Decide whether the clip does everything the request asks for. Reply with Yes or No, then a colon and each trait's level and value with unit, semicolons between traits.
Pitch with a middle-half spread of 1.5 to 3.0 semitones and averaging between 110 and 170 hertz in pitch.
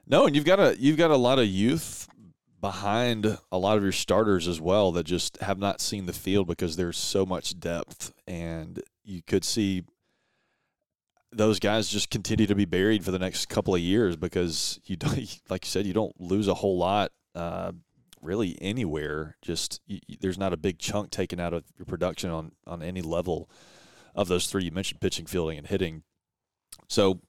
No: average, 2.7 semitones; very low, 95 Hz